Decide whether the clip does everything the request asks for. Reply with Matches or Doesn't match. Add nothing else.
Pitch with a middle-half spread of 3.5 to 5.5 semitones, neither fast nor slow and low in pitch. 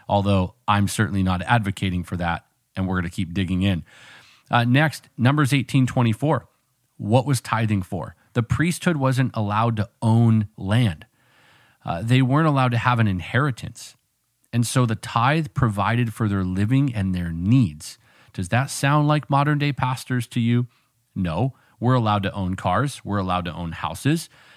Matches